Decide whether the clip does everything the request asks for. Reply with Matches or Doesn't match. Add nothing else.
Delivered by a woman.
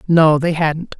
Doesn't match